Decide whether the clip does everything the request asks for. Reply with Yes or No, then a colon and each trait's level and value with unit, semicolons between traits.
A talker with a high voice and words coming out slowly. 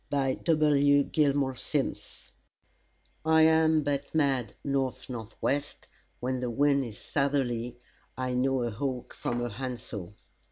No: low, 135 Hz; slow, 130 wpm